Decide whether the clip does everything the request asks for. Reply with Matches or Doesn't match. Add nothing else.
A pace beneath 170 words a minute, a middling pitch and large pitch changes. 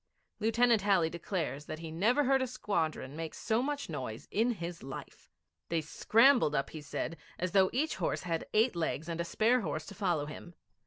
Doesn't match